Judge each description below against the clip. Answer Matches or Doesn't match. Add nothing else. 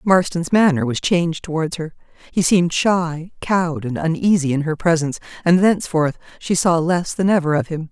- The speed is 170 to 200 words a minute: Matches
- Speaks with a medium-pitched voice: Matches